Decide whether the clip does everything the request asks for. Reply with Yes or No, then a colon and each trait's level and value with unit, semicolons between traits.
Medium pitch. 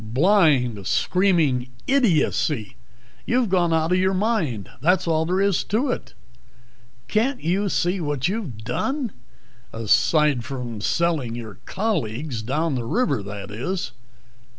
Yes: medium, 160 Hz